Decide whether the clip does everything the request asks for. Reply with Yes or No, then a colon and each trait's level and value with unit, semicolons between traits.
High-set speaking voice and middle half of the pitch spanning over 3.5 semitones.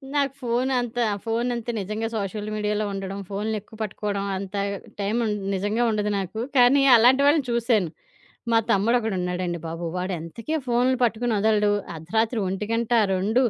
No: high, 215 Hz; average, 3.2 semitones